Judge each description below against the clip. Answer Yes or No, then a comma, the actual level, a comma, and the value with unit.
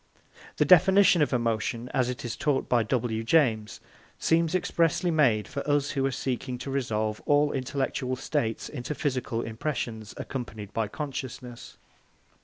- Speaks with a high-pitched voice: No, low, 130 Hz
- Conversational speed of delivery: Yes, average, 145 wpm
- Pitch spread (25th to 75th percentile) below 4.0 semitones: No, average, 4.3 semitones